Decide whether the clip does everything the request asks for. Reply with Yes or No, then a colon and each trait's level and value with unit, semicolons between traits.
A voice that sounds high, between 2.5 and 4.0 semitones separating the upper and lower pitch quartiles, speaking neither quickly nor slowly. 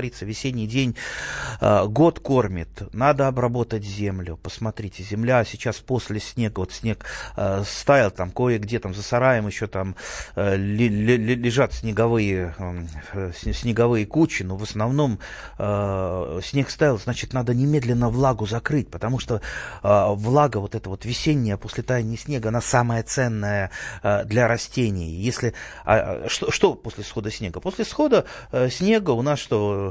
No: low, 115 Hz; average, 3.7 semitones; average, 130 wpm